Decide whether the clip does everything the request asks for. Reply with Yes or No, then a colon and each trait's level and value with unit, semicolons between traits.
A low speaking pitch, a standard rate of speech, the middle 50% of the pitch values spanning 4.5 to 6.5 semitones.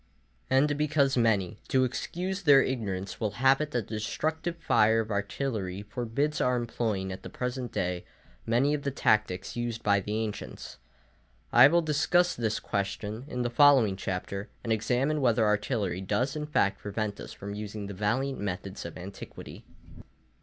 Yes: low, 115 Hz; average, 165 wpm; average, 5.0 semitones